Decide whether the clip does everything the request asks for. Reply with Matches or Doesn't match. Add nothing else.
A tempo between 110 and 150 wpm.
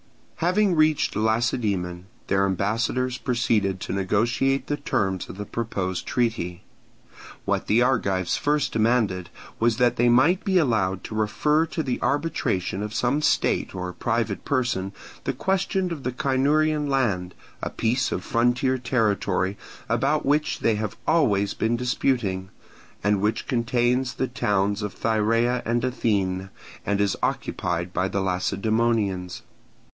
Matches